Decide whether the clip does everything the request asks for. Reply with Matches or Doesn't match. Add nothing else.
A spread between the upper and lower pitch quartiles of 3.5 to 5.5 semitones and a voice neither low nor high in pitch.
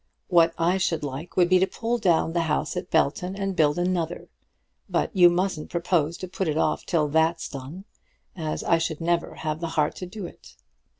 Doesn't match